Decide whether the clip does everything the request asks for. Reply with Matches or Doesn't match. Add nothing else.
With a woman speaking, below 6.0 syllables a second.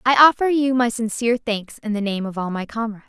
Doesn't match